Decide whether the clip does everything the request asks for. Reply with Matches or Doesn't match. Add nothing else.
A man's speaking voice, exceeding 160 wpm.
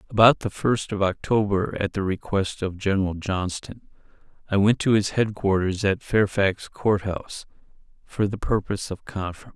Doesn't match